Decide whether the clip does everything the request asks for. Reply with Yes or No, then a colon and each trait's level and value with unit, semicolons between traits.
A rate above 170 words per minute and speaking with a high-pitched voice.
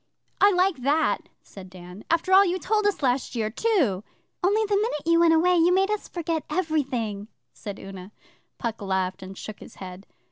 Yes: average, 185 wpm; very high, 300 Hz